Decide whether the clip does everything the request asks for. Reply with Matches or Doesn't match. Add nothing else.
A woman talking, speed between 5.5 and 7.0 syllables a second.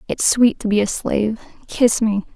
Doesn't match